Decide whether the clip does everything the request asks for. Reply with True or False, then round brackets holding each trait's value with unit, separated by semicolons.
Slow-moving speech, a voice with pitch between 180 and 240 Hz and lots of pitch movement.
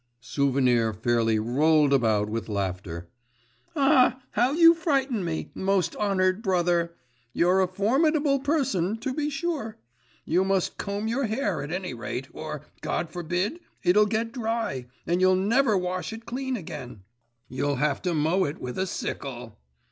False (150 wpm; 185 Hz; 8.6 semitones)